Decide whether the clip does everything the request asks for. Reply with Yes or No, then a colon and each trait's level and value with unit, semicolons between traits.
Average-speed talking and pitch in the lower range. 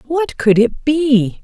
No: average, 170 wpm; very high, 265 Hz